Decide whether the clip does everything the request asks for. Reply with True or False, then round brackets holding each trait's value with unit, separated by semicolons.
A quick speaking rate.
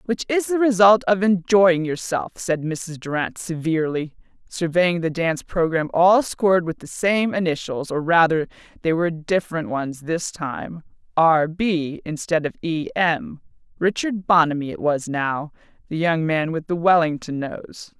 False (155 wpm)